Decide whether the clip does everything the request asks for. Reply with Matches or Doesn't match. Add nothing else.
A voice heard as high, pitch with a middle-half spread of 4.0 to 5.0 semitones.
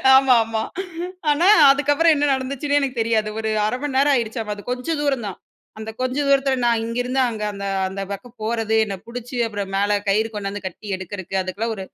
Matches